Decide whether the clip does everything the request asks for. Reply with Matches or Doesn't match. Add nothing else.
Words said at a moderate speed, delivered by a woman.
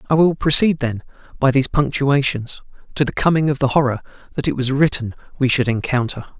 Doesn't match